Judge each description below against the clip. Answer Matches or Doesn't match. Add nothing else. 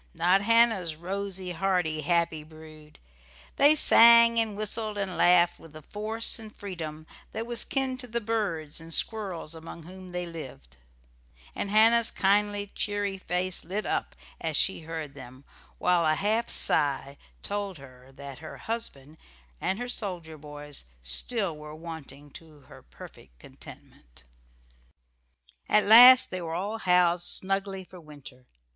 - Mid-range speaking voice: Matches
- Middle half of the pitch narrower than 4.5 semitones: Doesn't match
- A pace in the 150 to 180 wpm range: Doesn't match